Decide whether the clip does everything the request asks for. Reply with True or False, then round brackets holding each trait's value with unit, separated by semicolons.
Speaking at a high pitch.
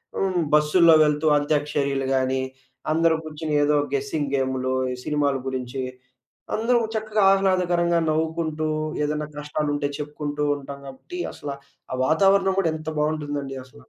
False (150 Hz)